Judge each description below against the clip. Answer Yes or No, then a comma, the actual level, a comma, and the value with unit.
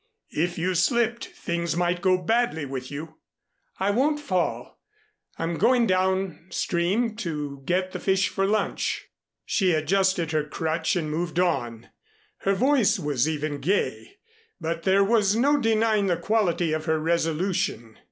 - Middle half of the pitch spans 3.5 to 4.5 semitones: Yes, average, 4.1 semitones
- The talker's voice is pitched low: No, medium, 180 Hz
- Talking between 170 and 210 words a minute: No, average, 145 wpm